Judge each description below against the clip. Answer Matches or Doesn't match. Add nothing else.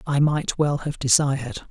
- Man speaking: Matches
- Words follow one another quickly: Doesn't match